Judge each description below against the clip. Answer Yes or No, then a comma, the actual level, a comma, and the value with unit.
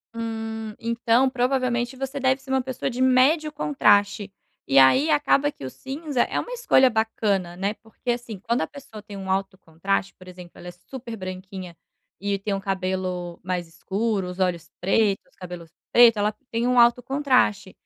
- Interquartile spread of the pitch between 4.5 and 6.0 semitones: Yes, average, 5.2 semitones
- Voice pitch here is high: Yes, high, 220 Hz